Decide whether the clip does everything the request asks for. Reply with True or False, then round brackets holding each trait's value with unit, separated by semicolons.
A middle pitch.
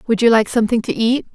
False (230 Hz)